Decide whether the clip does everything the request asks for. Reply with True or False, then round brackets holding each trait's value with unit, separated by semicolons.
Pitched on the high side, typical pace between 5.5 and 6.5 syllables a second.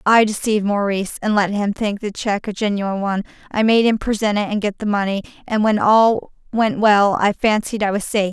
True (205 Hz; 5.6 syllables/s)